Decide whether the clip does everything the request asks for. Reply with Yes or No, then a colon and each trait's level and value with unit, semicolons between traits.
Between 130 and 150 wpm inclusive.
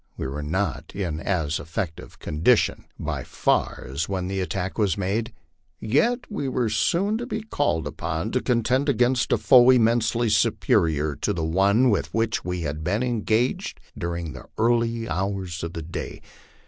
No: average, 165 wpm